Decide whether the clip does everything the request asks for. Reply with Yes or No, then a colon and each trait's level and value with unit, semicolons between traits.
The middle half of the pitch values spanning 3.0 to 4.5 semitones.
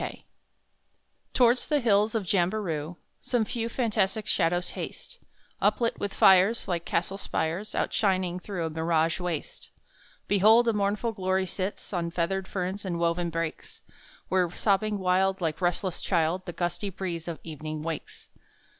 Yes: average, 3.3 semitones